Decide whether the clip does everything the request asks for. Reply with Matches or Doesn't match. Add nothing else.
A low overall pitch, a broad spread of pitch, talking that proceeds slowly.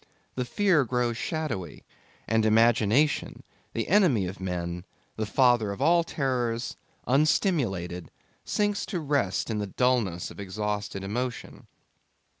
Matches